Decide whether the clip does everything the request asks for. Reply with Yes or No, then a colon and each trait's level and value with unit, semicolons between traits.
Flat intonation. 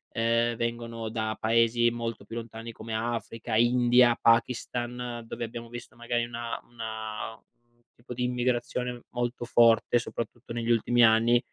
Yes: narrow, 0.9 semitones